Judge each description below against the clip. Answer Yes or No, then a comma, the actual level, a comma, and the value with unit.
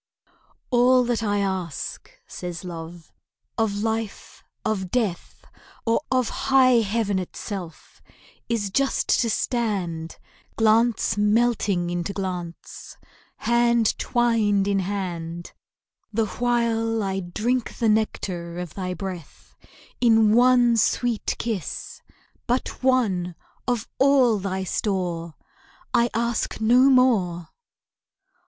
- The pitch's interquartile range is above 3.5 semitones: Yes, average, 4.5 semitones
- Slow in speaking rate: Yes, slow, 105 wpm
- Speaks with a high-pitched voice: Yes, high, 215 Hz